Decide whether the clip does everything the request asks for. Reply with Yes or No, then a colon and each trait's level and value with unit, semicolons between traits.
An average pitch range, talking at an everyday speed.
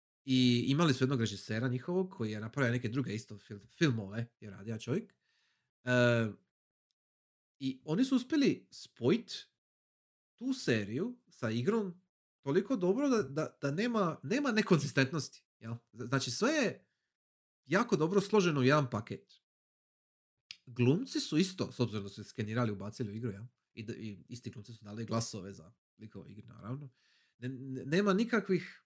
No: wide, 7.5 semitones; average, 145 wpm